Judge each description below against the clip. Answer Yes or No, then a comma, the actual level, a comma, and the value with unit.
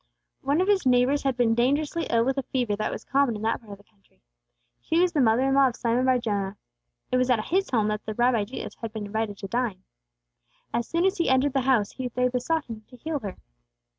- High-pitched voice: Yes, very high, 250 Hz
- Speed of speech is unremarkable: No, fast, 245 wpm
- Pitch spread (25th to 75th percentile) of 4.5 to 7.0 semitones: No, average, 3.8 semitones